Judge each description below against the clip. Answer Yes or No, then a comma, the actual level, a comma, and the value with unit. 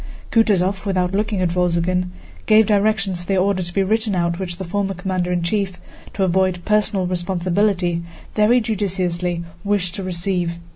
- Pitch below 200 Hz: Yes, medium, 185 Hz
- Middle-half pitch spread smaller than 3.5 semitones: Yes, narrow, 2.4 semitones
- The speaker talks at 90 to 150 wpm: No, average, 160 wpm